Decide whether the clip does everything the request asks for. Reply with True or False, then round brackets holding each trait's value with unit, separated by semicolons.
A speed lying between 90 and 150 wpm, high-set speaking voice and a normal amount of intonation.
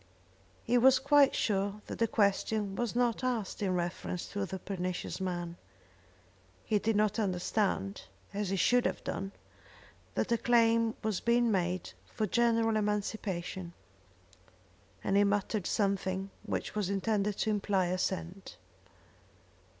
True (135 wpm; 205 Hz; 3.1 semitones)